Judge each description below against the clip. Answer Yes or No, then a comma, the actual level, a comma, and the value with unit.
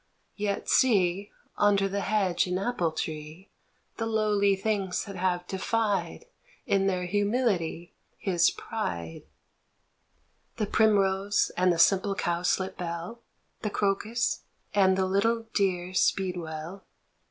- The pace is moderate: No, slow, 115 wpm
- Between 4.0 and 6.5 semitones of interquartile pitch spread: No, narrow, 2.6 semitones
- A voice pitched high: Yes, high, 195 Hz